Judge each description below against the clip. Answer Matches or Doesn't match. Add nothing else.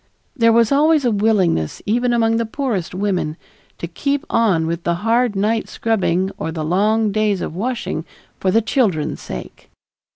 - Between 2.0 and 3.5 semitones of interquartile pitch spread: Doesn't match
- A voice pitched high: Matches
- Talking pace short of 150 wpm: Doesn't match